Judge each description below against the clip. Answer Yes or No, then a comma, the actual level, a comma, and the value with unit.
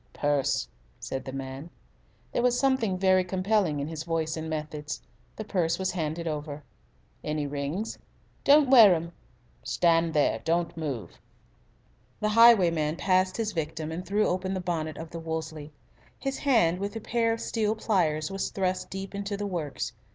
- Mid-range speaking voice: Yes, medium, 170 Hz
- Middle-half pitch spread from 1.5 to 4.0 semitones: No, average, 4.6 semitones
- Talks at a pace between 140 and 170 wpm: Yes, average, 165 wpm